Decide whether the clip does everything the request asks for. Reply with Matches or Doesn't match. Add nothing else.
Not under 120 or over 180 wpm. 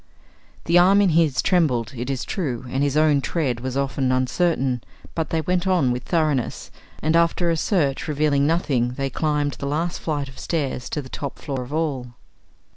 Doesn't match